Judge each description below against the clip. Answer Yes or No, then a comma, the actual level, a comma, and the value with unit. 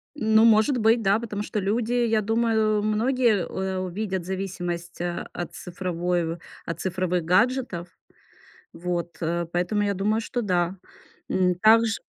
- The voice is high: Yes, high, 195 Hz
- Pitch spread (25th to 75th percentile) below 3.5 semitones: No, average, 3.8 semitones